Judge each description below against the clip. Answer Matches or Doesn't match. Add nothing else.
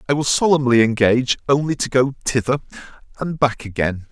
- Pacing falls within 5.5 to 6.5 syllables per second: Matches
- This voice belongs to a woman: Doesn't match